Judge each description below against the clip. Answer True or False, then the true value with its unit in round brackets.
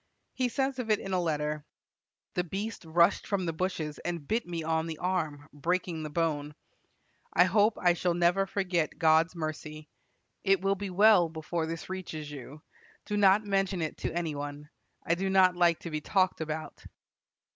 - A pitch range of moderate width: True (3.5 semitones)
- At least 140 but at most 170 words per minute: False (180 wpm)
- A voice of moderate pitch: True (175 Hz)